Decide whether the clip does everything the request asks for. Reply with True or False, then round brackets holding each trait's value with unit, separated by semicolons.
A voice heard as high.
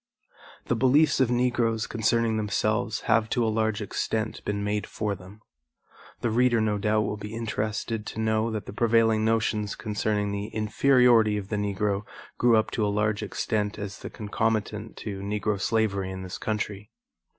False (110 Hz)